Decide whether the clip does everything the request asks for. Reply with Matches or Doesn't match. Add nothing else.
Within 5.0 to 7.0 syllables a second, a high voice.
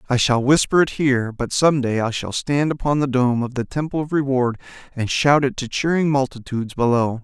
Doesn't match